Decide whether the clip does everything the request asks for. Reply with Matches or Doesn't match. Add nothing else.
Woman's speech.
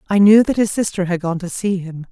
Matches